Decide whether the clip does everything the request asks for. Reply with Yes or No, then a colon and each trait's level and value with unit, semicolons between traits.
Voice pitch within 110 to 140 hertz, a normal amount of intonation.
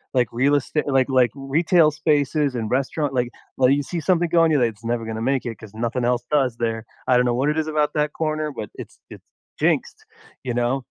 Yes: low, 135 Hz; average, 3.9 semitones